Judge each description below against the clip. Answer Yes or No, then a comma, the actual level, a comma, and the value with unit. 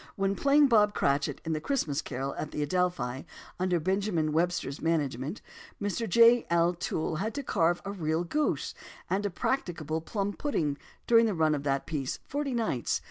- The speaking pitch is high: No, medium, 175 Hz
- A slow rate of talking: No, average, 180 wpm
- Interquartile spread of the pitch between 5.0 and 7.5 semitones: Yes, wide, 5.4 semitones